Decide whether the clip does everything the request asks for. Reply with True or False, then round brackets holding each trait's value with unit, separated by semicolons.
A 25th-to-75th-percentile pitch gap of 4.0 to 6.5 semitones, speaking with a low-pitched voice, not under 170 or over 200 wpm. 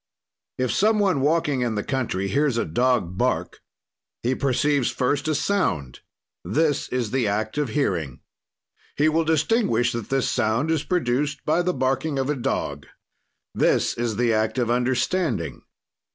False (4.6 semitones; 130 Hz; 155 wpm)